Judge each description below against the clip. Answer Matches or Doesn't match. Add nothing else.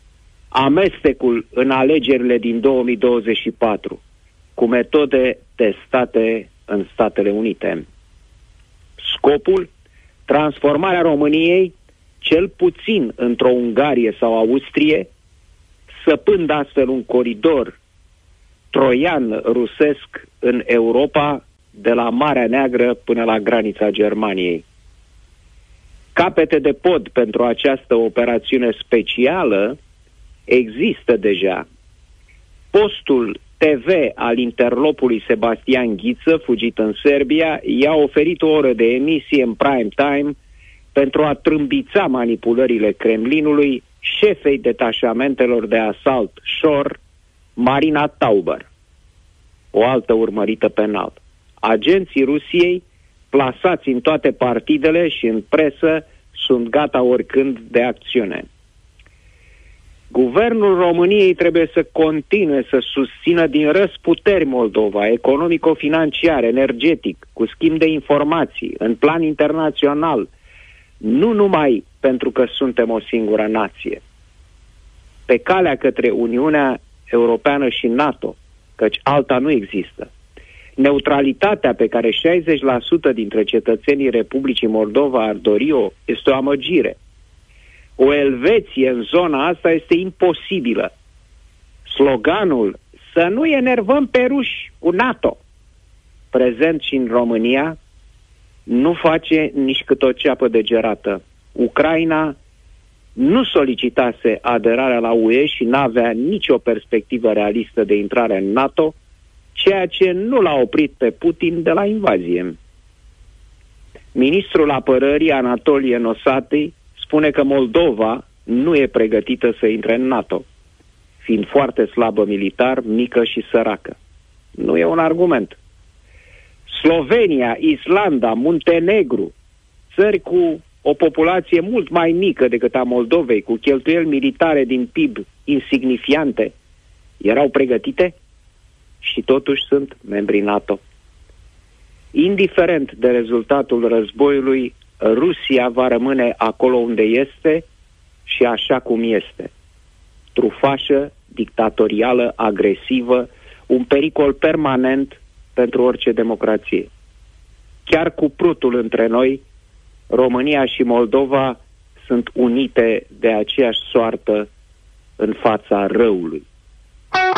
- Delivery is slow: Matches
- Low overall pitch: Matches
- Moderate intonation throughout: Doesn't match